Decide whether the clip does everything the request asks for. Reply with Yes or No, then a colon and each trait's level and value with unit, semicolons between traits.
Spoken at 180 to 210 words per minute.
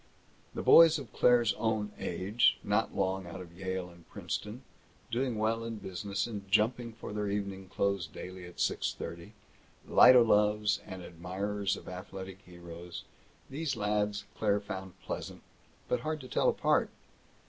No: average, 155 wpm